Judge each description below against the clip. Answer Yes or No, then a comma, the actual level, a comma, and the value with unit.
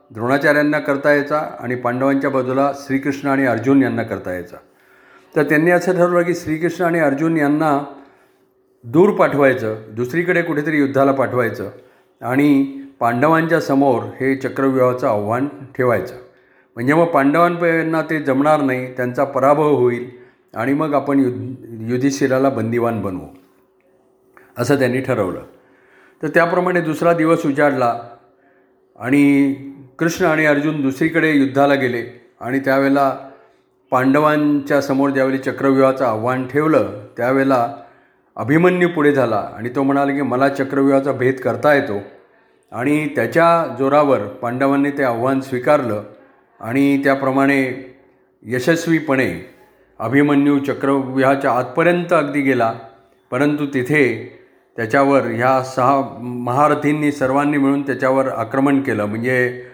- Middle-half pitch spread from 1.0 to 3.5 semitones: Yes, narrow, 2.4 semitones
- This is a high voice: No, low, 135 Hz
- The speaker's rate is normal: Yes, average, 115 wpm